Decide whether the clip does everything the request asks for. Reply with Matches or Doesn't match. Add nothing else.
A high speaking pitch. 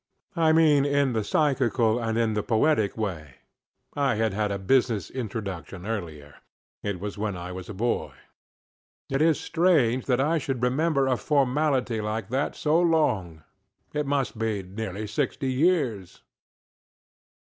Doesn't match